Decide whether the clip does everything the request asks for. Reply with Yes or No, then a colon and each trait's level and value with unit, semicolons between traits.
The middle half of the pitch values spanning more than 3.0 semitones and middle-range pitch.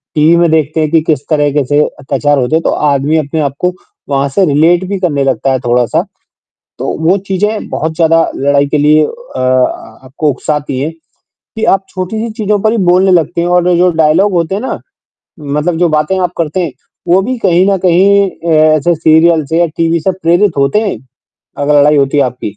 Yes: average, 3.6 semitones; medium, 160 Hz